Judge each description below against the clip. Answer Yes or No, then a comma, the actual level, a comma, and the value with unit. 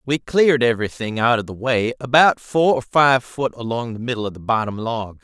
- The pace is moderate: No, fast, 220 wpm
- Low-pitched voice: Yes, low, 120 Hz